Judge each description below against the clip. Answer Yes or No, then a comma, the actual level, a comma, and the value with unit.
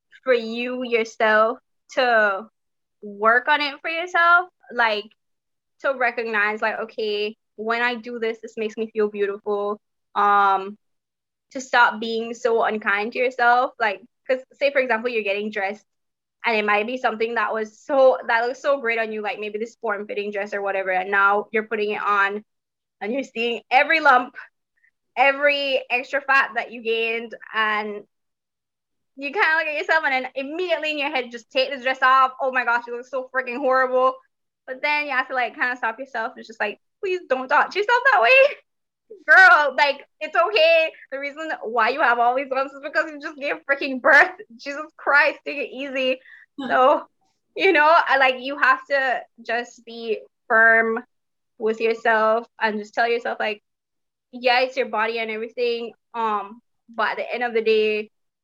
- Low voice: No, high, 240 Hz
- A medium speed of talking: Yes, average, 185 wpm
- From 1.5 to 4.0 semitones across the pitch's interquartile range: Yes, average, 3.7 semitones